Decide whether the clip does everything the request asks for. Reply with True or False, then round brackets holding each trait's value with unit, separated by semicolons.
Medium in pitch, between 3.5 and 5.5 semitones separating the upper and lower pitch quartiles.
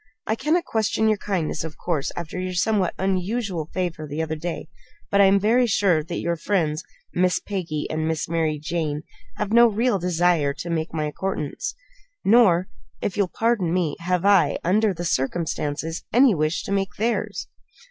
True (180 Hz; 4.1 semitones)